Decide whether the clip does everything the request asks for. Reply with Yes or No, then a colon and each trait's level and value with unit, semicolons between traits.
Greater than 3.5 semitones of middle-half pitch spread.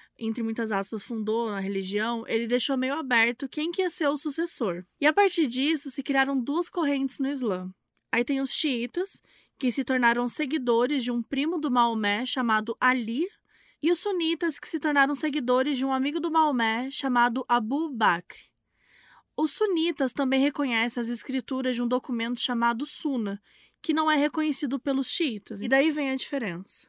Yes: average, 4.2 semitones